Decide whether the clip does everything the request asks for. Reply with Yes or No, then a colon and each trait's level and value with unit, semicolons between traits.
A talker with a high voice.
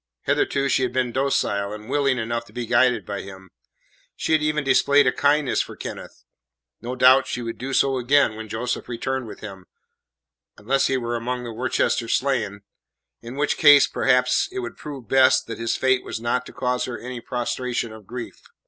No: low, 125 Hz